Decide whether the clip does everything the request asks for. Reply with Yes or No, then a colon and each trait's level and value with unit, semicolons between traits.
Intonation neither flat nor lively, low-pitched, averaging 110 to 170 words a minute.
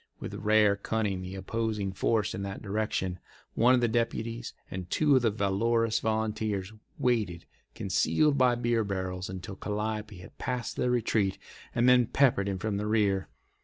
Yes: average, 3.1 semitones; low, 110 Hz; average, 160 wpm